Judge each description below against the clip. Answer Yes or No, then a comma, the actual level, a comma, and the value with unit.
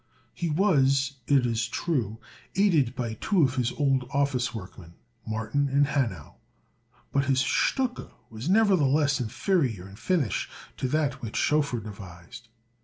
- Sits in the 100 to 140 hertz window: Yes, low, 135 Hz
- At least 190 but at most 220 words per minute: No, slow, 135 wpm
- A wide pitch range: No, average, 4.4 semitones